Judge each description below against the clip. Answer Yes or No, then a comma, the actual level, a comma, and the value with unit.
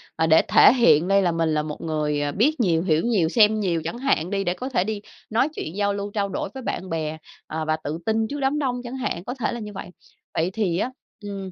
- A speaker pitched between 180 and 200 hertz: Yes, high, 195 Hz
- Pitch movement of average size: No, wide, 5.8 semitones